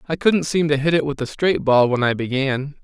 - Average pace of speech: No, fast, 275 wpm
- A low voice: No, medium, 145 Hz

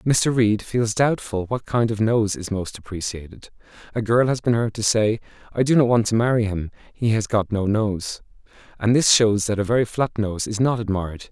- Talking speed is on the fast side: Yes, fast, 215 wpm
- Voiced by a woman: No, male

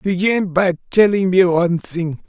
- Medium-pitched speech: Yes, medium, 180 Hz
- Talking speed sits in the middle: Yes, average, 160 wpm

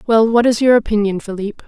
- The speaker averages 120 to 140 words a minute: No, fast, 215 wpm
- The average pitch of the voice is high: Yes, high, 220 Hz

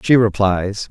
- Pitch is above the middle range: No, low, 105 Hz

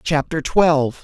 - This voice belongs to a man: Yes, male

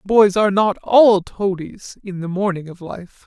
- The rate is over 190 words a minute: No, average, 185 wpm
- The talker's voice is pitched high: Yes, high, 195 Hz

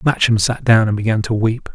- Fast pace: Yes, fast, 240 wpm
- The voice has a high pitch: No, low, 110 Hz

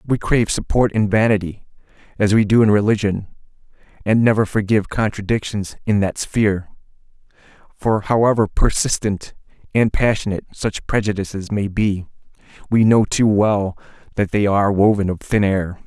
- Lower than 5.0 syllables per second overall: No, 5.3 syllables/s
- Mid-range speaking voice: No, low, 105 Hz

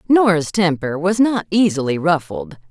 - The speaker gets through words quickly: No, slow, 135 wpm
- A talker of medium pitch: Yes, medium, 170 Hz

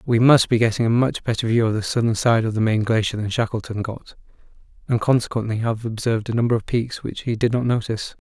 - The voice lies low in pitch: Yes, low, 115 Hz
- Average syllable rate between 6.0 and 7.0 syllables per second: Yes, 6.3 syllables/s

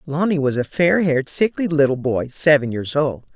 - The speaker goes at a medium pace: Yes, average, 195 wpm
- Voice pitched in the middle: Yes, medium, 150 Hz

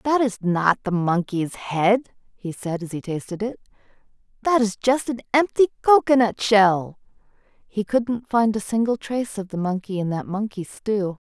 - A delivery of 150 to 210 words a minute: Yes, average, 170 wpm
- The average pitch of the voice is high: Yes, high, 210 Hz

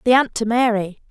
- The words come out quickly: Yes, fast, 215 wpm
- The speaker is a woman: Yes, female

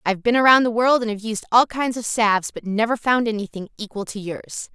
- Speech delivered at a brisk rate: Yes, fast, 255 wpm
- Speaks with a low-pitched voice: No, high, 225 Hz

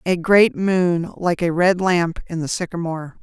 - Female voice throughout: Yes, female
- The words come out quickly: No, average, 185 wpm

